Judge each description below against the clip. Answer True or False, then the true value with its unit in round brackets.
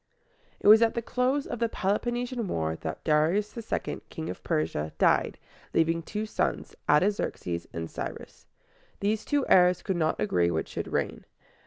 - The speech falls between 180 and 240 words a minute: False (160 wpm)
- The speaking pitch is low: False (190 Hz)